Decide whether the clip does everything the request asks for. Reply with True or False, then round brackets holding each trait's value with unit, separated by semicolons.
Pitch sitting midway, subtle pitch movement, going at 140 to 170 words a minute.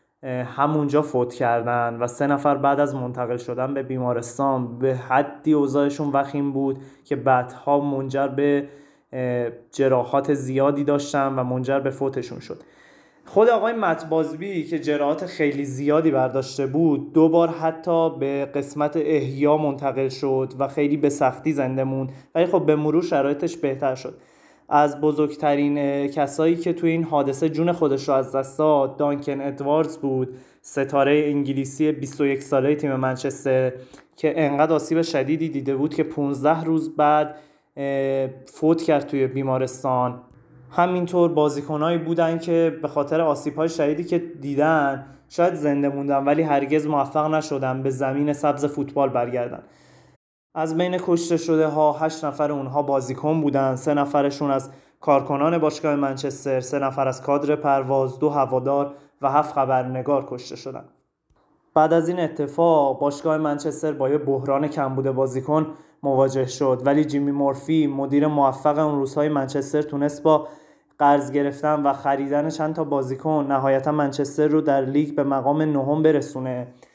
True (145 Hz; 2.1 semitones; 145 wpm)